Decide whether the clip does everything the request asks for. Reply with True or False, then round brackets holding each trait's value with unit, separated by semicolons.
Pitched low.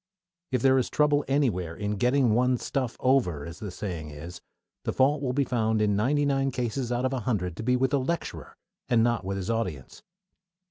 True (120 Hz)